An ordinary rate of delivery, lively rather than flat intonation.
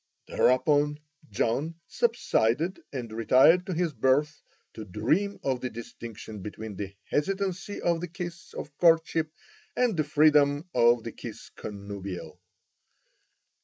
No: slow, 125 wpm; wide, 6.8 semitones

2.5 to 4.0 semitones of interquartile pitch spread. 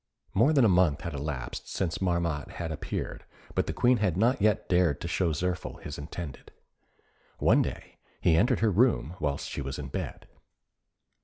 No: average, 5.2 semitones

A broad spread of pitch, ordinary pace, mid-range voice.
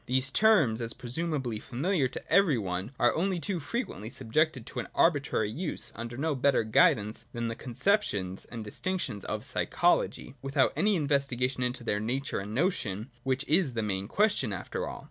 No: wide, 5.8 semitones; average, 170 wpm; low, 130 Hz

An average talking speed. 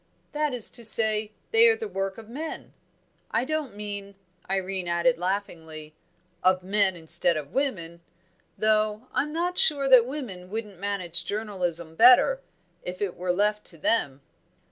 Yes: average, 150 wpm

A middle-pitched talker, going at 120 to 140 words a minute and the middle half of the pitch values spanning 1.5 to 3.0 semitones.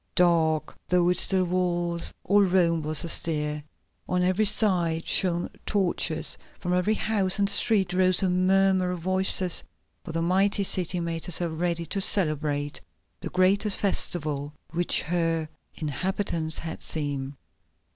Yes: medium, 175 Hz; slow, 135 wpm; narrow, 2.6 semitones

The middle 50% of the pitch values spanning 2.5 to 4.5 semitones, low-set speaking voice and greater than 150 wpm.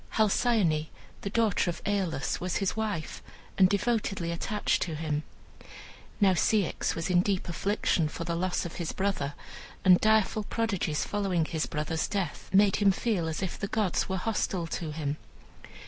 No: average, 3.8 semitones; medium, 185 Hz; average, 165 wpm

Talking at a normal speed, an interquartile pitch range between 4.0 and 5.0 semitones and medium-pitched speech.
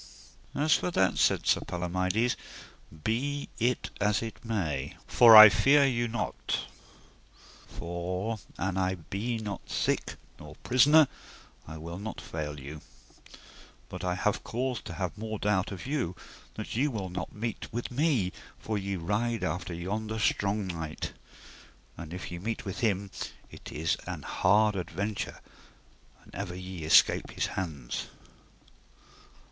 No: average, 145 wpm; average, 4.3 semitones; low, 100 Hz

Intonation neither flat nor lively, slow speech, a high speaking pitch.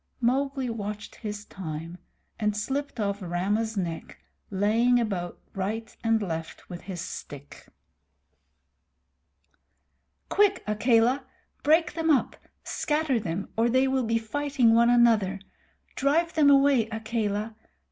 Yes: average, 4.8 semitones; slow, 120 wpm; high, 225 Hz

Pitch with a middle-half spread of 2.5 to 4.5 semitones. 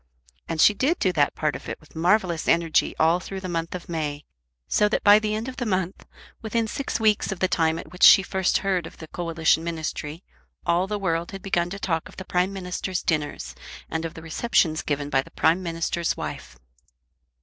Yes: average, 3.3 semitones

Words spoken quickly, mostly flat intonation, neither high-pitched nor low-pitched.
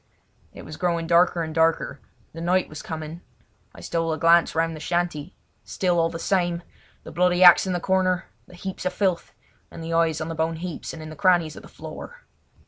Yes: fast, 215 wpm; narrow, 1.7 semitones; medium, 170 Hz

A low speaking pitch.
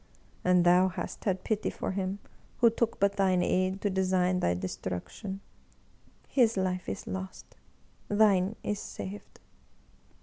No: high, 190 Hz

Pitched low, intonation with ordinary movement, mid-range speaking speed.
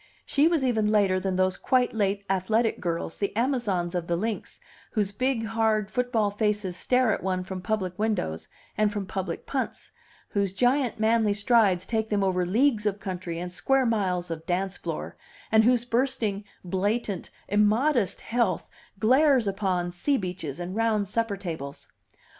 No: high, 205 Hz; average, 3.6 semitones; average, 160 wpm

